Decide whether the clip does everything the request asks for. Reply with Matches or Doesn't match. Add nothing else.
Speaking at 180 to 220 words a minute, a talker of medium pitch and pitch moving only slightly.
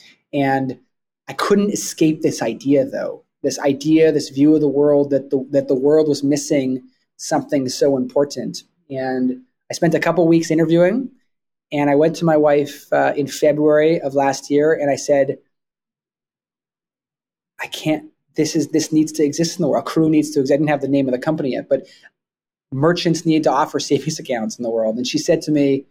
Matches